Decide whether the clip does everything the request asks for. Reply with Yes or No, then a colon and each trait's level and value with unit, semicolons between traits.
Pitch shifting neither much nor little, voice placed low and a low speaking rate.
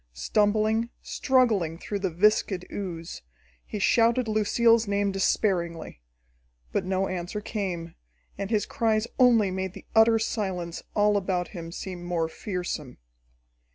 No: average, 3.6 semitones; high, 200 Hz; slow, 125 wpm